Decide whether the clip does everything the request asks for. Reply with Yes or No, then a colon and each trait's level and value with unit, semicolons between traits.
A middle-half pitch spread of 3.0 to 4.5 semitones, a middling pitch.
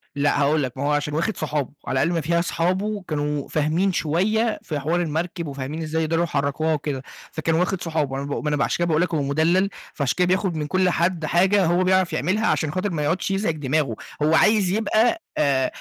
Yes: average, 3.7 semitones; medium, 160 Hz